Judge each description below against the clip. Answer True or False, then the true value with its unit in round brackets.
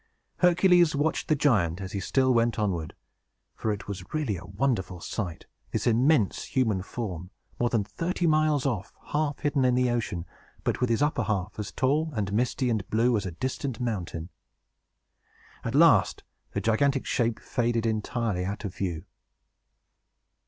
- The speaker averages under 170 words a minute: True (160 wpm)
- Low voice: True (115 Hz)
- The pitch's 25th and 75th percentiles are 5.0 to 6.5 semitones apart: True (5.6 semitones)